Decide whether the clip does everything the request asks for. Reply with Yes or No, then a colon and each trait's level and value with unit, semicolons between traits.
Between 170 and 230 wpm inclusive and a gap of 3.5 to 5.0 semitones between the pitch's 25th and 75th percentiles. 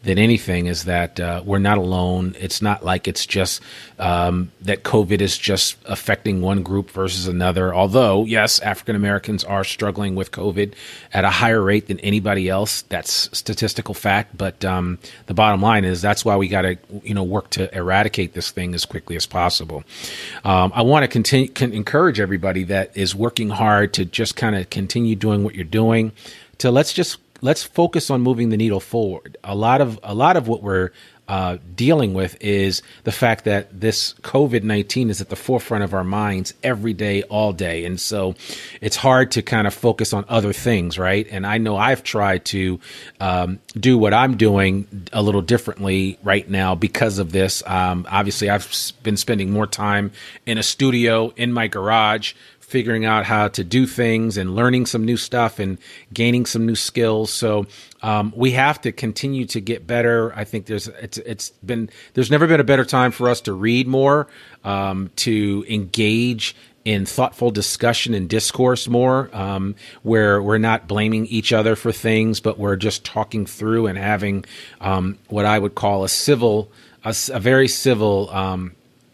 No: average, 185 wpm; average, 2.9 semitones